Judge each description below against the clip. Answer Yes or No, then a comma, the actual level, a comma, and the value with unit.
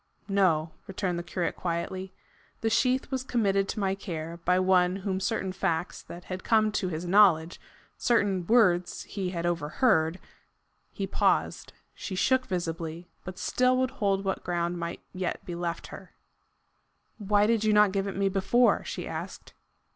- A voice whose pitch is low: No, high, 190 Hz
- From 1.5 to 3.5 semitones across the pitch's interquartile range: Yes, average, 3.1 semitones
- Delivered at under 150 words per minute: No, average, 165 wpm